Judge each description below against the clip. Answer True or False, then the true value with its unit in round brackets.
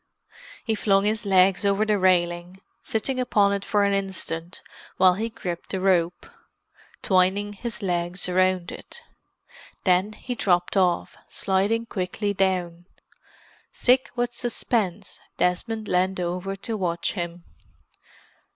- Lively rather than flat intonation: False (2.7 semitones)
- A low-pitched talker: False (190 Hz)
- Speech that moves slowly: True (125 wpm)